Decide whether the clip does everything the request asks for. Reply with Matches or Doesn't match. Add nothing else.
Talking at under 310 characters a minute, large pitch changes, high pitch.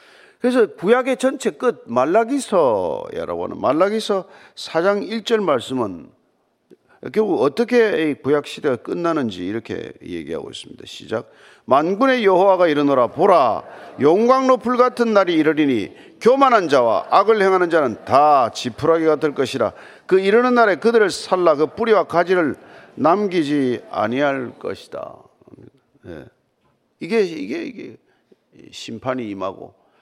Matches